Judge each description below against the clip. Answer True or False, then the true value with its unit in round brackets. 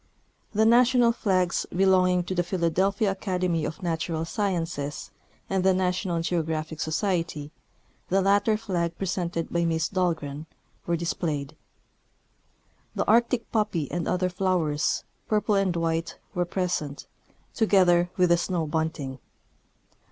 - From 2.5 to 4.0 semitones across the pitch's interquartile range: True (2.8 semitones)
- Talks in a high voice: False (175 Hz)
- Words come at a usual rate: False (120 wpm)